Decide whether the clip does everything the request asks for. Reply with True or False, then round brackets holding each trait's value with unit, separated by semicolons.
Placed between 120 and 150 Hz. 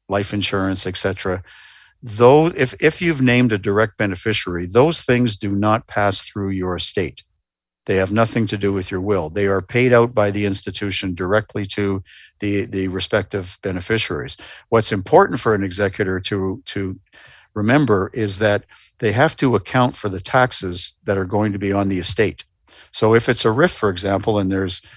False (100 Hz)